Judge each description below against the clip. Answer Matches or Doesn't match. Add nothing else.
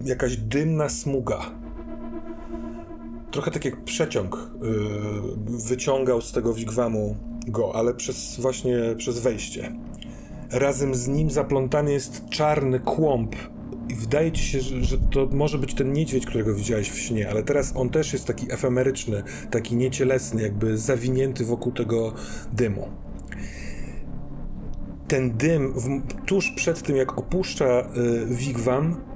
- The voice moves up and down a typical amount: Matches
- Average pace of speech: Matches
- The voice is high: Doesn't match